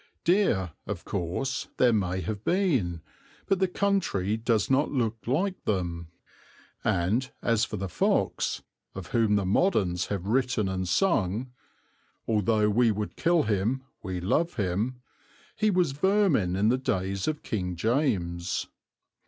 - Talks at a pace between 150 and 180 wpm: No, average, 140 wpm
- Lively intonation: Yes, wide, 6.3 semitones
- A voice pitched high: No, low, 110 Hz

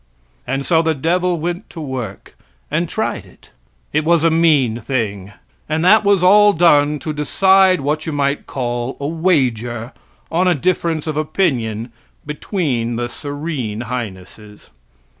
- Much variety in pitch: Yes, wide, 5.8 semitones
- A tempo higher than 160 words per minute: No, average, 145 wpm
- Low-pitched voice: No, medium, 150 Hz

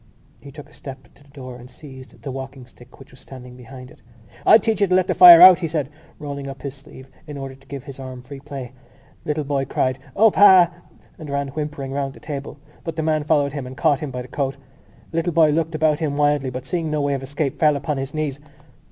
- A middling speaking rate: No, fast, 250 wpm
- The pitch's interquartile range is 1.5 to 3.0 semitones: Yes, narrow, 2.6 semitones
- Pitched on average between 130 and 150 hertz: Yes, medium, 140 Hz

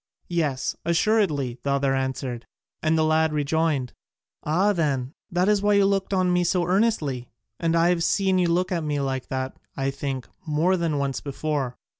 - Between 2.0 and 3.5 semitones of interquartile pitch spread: No, average, 4.7 semitones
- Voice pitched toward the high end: No, medium, 155 Hz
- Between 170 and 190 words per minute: Yes, average, 180 wpm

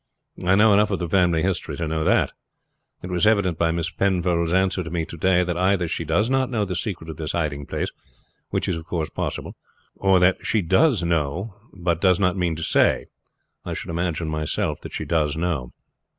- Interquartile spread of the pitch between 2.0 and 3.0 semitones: Yes, narrow, 2.6 semitones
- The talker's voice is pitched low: Yes, very low, 90 Hz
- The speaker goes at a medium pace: No, fast, 215 wpm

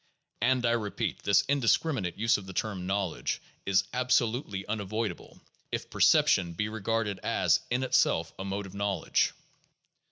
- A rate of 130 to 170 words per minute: Yes, average, 140 wpm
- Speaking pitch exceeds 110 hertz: No, low, 105 Hz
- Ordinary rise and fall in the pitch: Yes, average, 3.3 semitones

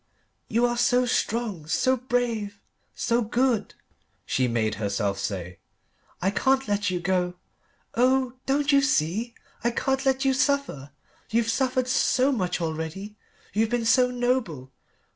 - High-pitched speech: Yes, high, 230 Hz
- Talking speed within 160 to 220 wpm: No, average, 140 wpm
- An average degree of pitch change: No, wide, 6.4 semitones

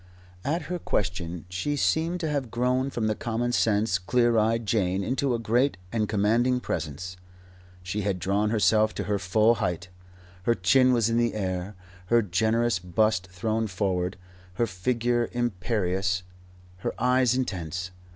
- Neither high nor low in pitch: No, low, 110 Hz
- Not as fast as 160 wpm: Yes, average, 150 wpm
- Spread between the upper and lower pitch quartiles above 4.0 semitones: Yes, average, 4.5 semitones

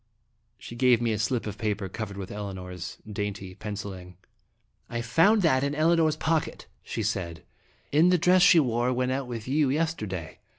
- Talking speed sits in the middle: Yes, average, 175 wpm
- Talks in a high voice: No, low, 120 Hz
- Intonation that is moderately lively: No, wide, 7.1 semitones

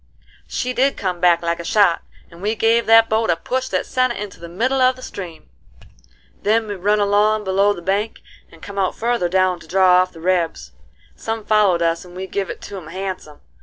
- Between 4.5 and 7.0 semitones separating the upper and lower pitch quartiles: No, average, 3.8 semitones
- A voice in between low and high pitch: No, high, 195 Hz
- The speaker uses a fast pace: Yes, fast, 220 wpm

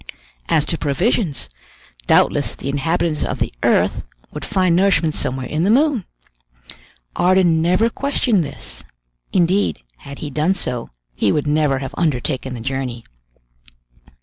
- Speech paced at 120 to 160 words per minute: Yes, slow, 135 wpm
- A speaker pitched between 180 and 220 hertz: No, medium, 160 Hz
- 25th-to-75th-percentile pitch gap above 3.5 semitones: Yes, average, 5.3 semitones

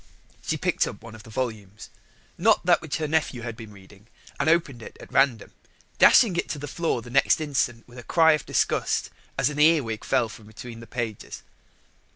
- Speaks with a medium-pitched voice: No, low, 125 Hz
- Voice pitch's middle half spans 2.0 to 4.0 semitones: No, wide, 5.5 semitones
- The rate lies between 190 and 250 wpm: Yes, average, 200 wpm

